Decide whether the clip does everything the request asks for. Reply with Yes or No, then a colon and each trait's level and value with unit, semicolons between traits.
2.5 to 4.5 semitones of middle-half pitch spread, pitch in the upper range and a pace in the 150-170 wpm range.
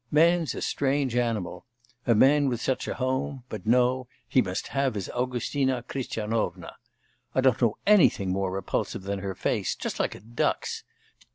No: average, 4.0 semitones; low, 125 Hz; average, 165 wpm